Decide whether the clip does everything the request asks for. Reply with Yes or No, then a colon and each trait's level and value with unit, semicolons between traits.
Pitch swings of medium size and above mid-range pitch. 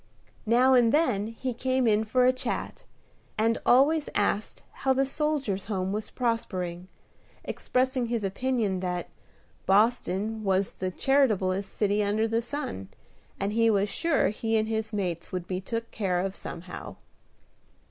Yes: average, 4.5 semitones; high, 220 Hz